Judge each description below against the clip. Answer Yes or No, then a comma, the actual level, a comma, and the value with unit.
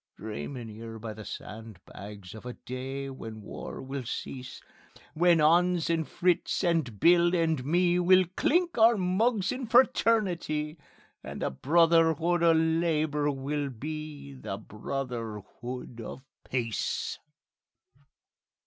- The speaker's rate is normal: No, slow, 120 wpm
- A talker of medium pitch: Yes, medium, 150 Hz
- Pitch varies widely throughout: Yes, wide, 6.1 semitones